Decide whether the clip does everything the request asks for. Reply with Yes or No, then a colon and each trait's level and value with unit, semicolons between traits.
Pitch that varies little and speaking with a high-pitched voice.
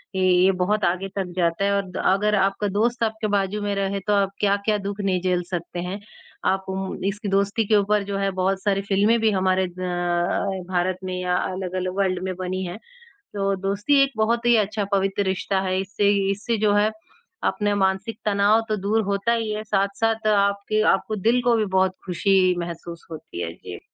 Yes: narrow, 2.0 semitones; high, 200 Hz